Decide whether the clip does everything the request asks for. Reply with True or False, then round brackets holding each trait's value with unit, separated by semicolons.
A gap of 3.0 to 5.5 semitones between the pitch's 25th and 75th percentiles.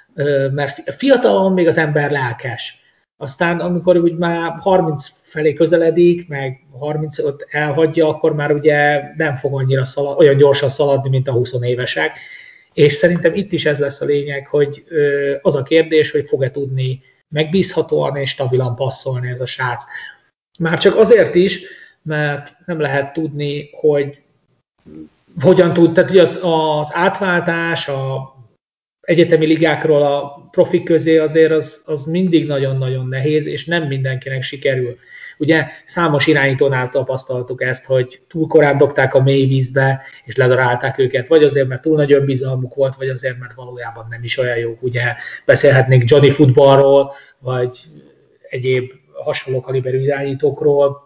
True (3.3 semitones)